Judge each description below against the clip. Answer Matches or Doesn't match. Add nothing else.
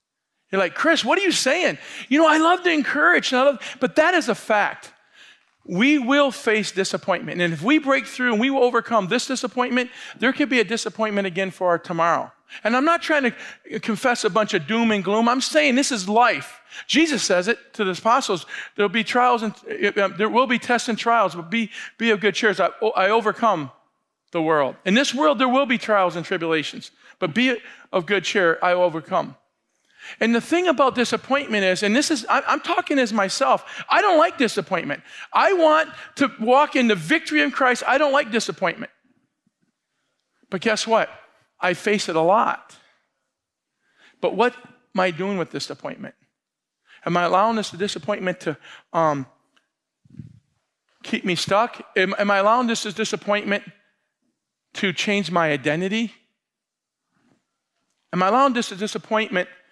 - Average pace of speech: Matches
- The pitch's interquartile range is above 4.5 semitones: Matches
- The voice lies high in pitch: Matches